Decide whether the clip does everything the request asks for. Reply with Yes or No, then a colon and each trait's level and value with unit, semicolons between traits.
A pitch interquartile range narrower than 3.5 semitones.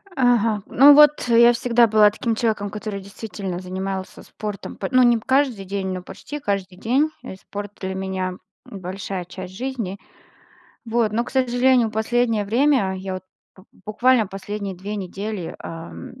No: average, 4.0 semitones